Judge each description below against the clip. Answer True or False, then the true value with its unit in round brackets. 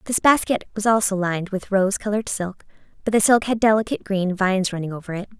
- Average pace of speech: False (210 wpm)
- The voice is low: False (200 Hz)